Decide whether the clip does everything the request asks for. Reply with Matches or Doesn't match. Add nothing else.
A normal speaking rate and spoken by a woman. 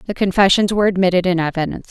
Matches